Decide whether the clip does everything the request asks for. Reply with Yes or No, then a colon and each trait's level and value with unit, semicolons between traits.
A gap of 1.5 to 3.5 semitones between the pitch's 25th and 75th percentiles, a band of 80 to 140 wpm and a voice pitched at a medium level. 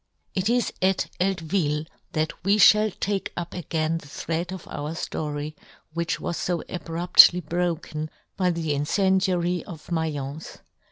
Yes: average, 2.9 semitones; slow, 135 wpm; medium, 170 Hz